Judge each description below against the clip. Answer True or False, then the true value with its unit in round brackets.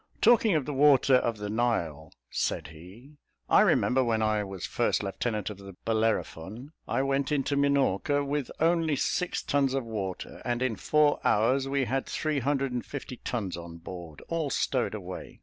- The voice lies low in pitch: True (125 Hz)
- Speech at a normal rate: True (175 wpm)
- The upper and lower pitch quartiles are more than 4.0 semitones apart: True (5.3 semitones)